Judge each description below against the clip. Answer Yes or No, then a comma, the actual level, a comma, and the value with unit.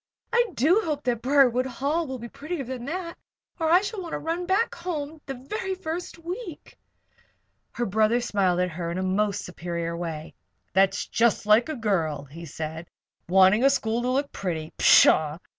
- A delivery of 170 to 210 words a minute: Yes, average, 175 wpm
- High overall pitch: Yes, high, 245 Hz